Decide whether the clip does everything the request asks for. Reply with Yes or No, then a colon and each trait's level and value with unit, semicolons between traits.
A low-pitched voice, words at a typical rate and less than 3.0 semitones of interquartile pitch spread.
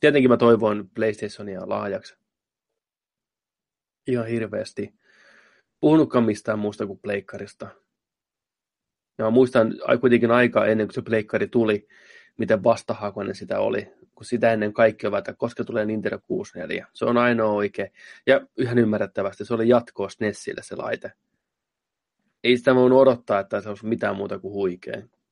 Yes: low, 115 Hz; average, 135 wpm; narrow, 2.5 semitones